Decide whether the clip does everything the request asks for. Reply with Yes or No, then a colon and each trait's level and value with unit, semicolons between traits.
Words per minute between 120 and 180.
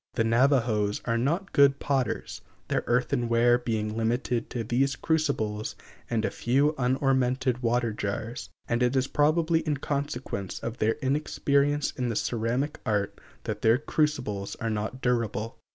Yes: average, 145 wpm